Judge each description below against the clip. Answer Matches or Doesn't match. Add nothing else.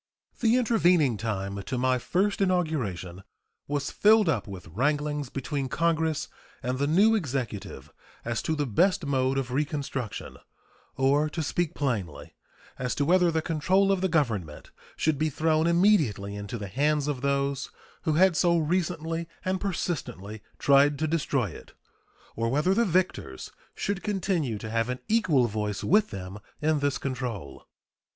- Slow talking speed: Doesn't match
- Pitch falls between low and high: Matches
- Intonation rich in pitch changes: Matches